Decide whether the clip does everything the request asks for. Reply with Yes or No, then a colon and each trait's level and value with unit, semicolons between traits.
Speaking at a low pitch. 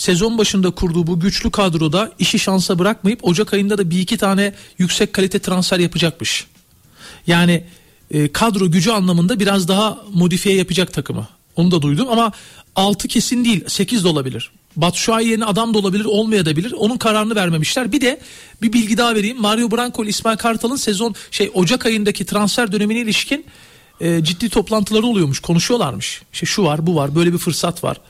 No: high, 200 Hz